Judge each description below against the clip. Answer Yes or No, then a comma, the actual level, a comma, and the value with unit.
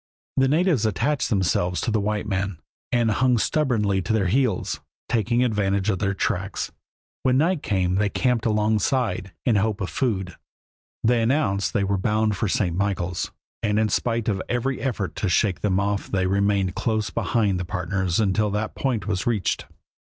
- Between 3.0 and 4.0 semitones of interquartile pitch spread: Yes, average, 3.3 semitones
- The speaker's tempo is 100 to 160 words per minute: No, average, 180 wpm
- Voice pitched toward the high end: No, low, 105 Hz